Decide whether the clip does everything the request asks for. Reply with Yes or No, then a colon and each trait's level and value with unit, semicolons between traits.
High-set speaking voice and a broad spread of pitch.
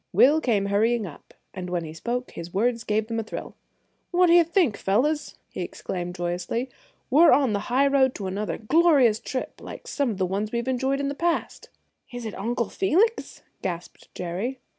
Yes: high, 235 Hz; wide, 5.9 semitones